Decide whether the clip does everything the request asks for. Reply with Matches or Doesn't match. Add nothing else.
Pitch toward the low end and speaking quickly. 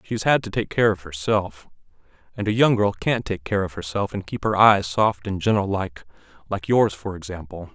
Matches